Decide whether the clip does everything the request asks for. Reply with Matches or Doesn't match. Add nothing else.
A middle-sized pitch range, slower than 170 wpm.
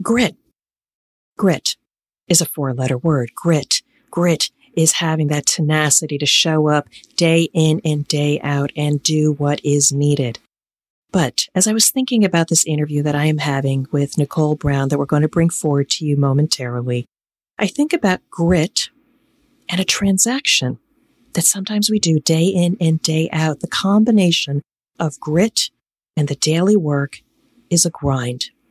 Matches